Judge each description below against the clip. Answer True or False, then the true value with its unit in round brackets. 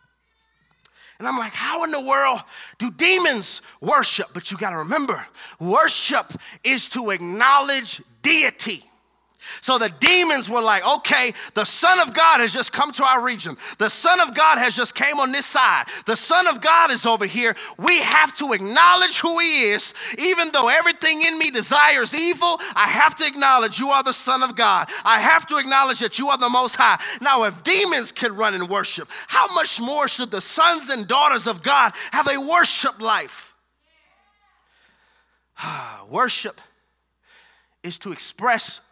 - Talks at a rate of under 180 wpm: True (170 wpm)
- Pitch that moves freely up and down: True (5.8 semitones)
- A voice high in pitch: True (275 Hz)